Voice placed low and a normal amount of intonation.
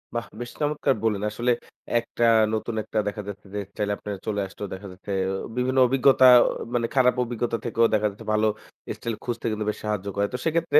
Yes: low, 115 Hz; average, 3.2 semitones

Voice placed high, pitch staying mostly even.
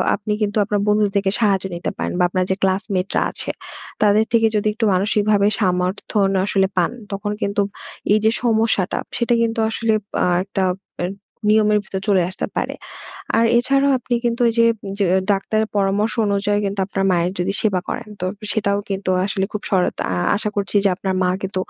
Yes: high, 205 Hz; narrow, 1.9 semitones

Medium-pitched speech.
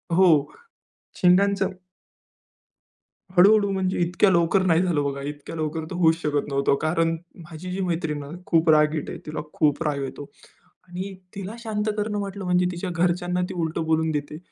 Yes: medium, 170 Hz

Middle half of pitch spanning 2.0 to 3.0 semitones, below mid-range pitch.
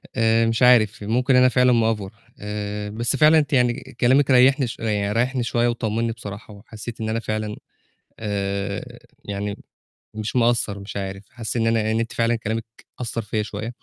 Yes: narrow, 2.5 semitones; low, 115 Hz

